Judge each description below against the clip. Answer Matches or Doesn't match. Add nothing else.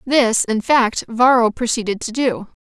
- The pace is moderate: Matches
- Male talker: Doesn't match